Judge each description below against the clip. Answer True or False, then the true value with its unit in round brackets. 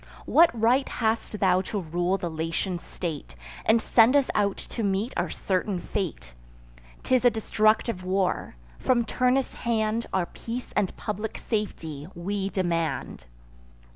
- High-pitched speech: True (200 Hz)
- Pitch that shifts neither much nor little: True (4.2 semitones)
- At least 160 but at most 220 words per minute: False (140 wpm)